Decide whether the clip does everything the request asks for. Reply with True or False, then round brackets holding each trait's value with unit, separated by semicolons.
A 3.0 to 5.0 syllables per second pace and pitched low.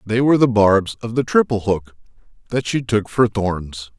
True (4.7 syllables/s; 110 Hz)